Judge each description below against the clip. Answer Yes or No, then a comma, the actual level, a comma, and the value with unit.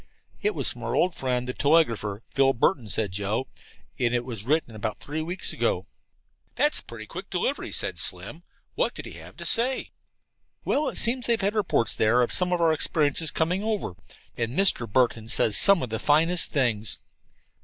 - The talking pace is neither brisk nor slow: Yes, average, 185 wpm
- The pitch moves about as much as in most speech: No, wide, 7.9 semitones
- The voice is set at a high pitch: No, medium, 140 Hz